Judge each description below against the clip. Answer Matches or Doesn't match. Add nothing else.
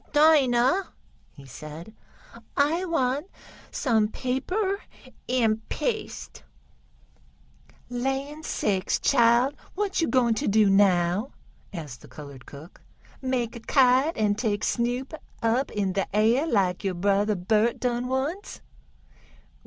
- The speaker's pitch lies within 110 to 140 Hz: Doesn't match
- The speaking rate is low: Matches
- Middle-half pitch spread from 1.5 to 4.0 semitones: Doesn't match